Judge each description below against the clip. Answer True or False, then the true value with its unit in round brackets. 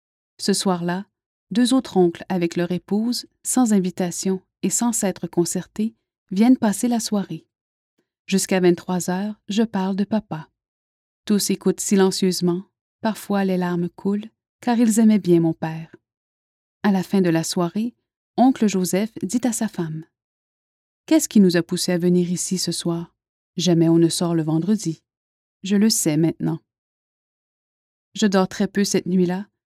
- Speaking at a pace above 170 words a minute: False (155 wpm)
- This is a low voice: False (185 Hz)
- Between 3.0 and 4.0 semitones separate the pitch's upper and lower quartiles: True (3.3 semitones)